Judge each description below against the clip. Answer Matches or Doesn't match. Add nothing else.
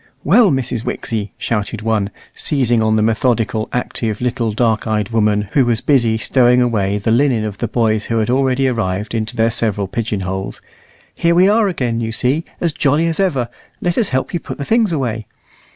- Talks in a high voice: Doesn't match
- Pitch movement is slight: Doesn't match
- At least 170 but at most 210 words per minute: Matches